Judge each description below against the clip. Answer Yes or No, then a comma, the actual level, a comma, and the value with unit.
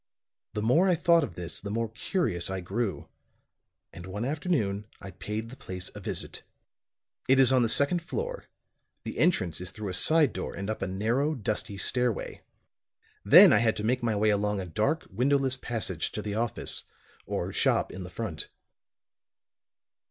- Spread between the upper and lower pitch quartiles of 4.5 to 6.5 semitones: Yes, average, 5.2 semitones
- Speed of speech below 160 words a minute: No, average, 175 wpm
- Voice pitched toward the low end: Yes, low, 110 Hz